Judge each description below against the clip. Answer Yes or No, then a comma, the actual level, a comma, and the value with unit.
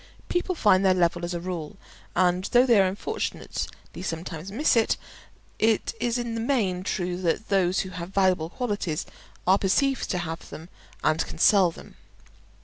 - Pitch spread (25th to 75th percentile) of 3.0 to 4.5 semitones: Yes, average, 4.1 semitones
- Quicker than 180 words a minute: No, average, 165 wpm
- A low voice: No, medium, 185 Hz